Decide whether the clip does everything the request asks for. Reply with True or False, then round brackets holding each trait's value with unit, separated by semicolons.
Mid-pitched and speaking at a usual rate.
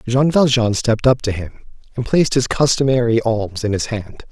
False (120 Hz; 195 wpm)